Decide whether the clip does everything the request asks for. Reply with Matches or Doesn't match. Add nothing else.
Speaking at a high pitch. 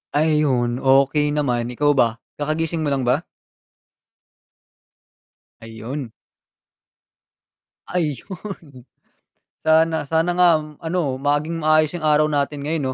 Doesn't match